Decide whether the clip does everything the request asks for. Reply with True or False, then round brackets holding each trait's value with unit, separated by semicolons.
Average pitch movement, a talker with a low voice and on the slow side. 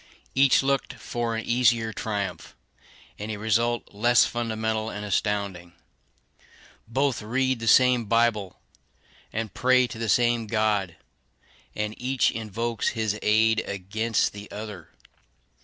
False (2.2 semitones; 110 Hz; 125 wpm)